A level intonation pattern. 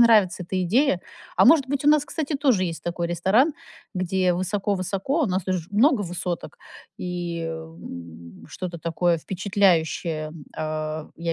No: average, 3.7 semitones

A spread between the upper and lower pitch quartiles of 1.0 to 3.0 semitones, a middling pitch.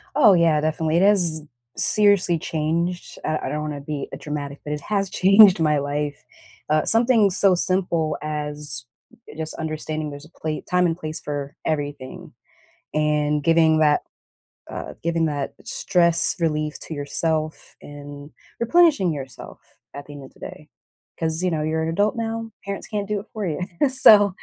No: average, 3.6 semitones; medium, 160 Hz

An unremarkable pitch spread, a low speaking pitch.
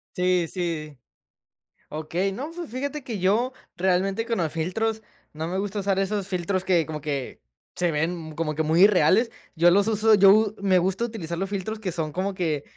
No: average, 4.0 semitones; medium, 185 Hz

